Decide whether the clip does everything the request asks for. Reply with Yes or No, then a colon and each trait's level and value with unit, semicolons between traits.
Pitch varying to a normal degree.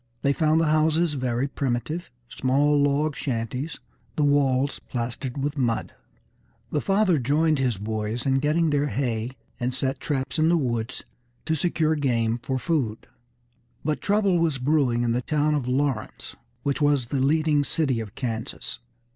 Yes: average, 3.7 semitones